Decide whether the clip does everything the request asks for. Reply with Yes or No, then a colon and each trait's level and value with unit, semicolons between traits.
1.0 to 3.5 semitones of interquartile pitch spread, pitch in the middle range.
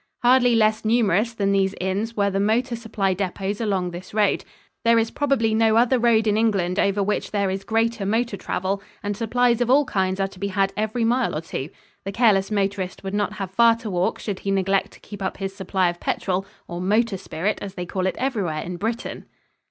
No: average, 2.9 semitones; high, 205 Hz